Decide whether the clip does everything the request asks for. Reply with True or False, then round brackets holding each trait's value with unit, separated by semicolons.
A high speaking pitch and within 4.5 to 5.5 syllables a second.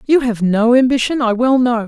True (240 Hz; 5.3 syllables/s)